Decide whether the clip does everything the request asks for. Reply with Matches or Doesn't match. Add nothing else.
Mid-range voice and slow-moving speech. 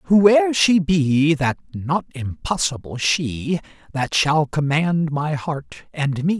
Matches